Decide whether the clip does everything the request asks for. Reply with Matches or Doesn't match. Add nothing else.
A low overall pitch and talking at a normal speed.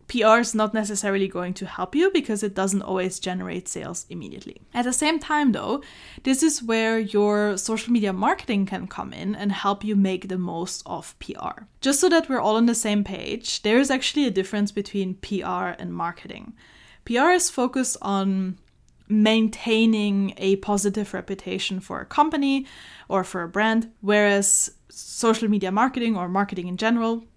Doesn't match